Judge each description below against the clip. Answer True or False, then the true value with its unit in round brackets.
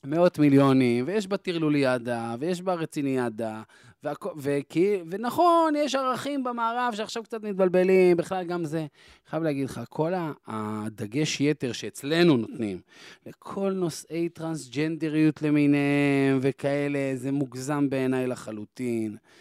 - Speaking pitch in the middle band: True (150 Hz)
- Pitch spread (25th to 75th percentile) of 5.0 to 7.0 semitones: True (5.5 semitones)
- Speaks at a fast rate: False (115 wpm)